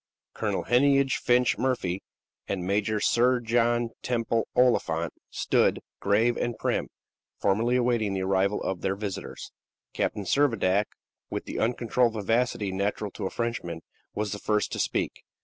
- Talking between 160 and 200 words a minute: No, average, 140 wpm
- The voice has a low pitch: Yes, low, 110 Hz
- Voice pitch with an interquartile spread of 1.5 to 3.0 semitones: No, average, 3.6 semitones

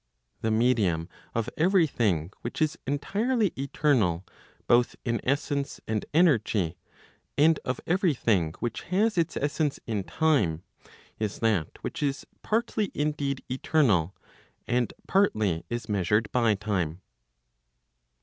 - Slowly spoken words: Yes, slow, 120 wpm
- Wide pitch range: Yes, wide, 7.1 semitones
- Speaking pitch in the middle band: No, low, 125 Hz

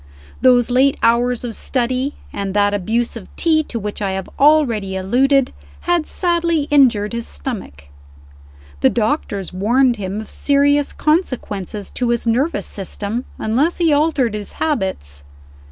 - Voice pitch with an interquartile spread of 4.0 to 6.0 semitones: Yes, wide, 5.6 semitones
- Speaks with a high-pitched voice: Yes, high, 240 Hz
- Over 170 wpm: No, average, 140 wpm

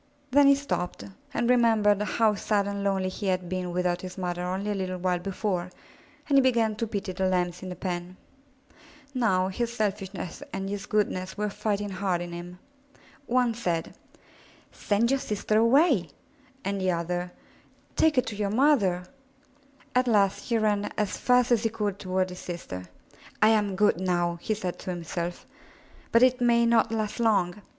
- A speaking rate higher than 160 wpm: Yes, average, 175 wpm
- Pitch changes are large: No, average, 3.7 semitones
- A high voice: Yes, high, 200 Hz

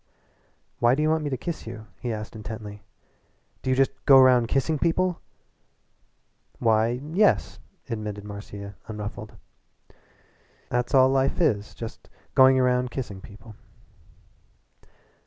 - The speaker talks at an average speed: No, slow, 125 wpm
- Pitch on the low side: Yes, low, 125 Hz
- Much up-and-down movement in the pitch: No, average, 3.9 semitones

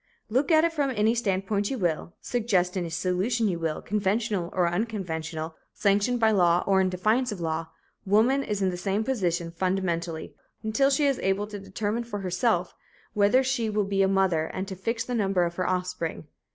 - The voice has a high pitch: Yes, high, 195 Hz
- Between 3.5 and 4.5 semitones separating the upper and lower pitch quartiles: Yes, average, 3.9 semitones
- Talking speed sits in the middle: Yes, average, 190 wpm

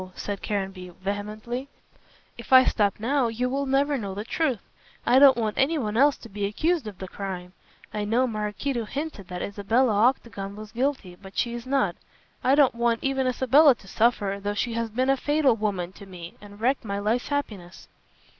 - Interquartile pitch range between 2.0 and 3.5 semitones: No, average, 4.5 semitones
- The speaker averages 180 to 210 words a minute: Yes, average, 190 wpm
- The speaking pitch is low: No, high, 230 Hz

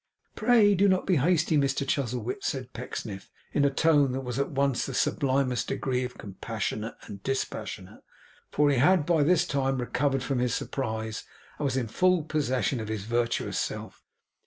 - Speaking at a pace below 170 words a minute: No, average, 175 wpm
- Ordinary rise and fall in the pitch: Yes, average, 3.3 semitones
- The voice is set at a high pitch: No, low, 135 Hz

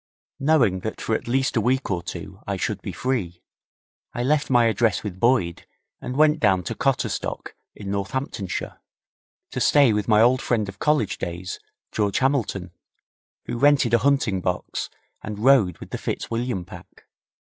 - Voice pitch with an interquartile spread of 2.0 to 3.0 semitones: No, average, 5.3 semitones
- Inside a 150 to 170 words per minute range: Yes, average, 165 wpm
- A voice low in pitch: Yes, low, 115 Hz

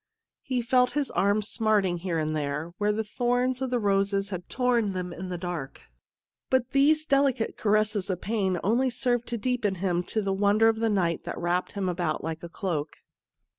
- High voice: Yes, high, 205 Hz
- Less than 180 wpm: No, average, 195 wpm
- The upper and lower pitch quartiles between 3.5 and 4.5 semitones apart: No, average, 5.2 semitones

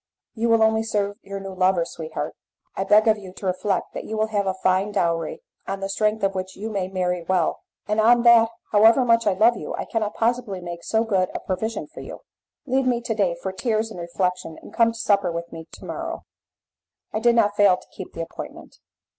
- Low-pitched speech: No, high, 205 Hz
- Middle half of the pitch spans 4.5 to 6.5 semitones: No, average, 3.2 semitones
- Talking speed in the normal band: No, fast, 220 wpm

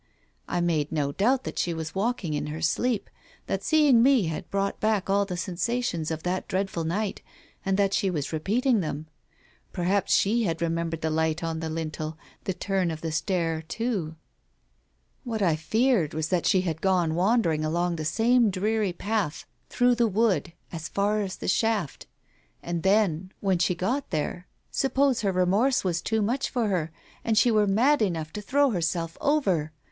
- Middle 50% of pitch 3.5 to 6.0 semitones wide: Yes, average, 5.1 semitones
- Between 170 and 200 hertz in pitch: Yes, medium, 185 Hz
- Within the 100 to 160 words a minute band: No, average, 185 wpm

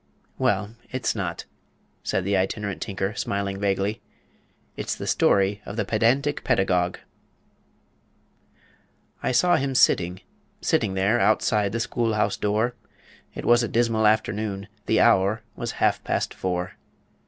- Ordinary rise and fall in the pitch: Yes, average, 3.0 semitones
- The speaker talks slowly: Yes, slow, 130 wpm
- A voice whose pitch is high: No, low, 105 Hz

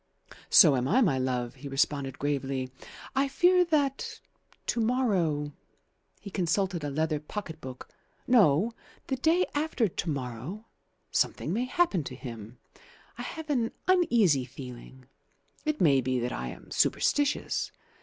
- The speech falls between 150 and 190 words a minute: No, average, 140 wpm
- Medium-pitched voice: Yes, medium, 160 Hz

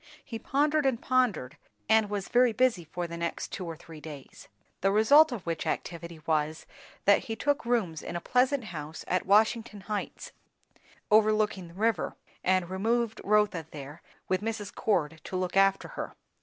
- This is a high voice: Yes, high, 200 Hz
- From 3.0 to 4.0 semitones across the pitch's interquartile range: No, average, 4.9 semitones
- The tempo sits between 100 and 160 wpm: No, average, 170 wpm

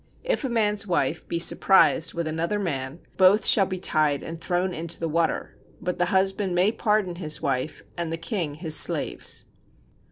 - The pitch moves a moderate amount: Yes, average, 3.0 semitones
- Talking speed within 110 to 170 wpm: No, average, 180 wpm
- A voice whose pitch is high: No, medium, 175 Hz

